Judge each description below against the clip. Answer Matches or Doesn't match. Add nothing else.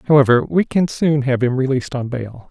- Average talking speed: Doesn't match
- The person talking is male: Matches